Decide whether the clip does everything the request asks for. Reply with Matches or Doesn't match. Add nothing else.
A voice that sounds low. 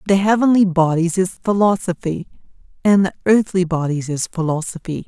Doesn't match